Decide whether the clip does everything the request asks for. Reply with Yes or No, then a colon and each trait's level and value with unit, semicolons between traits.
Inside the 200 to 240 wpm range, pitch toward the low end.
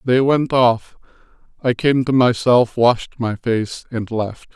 No: average, 160 wpm; low, 120 Hz